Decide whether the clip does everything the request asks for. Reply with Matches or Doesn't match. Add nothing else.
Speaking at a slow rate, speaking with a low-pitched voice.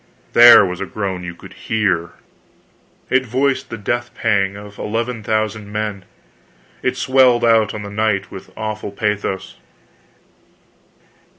Matches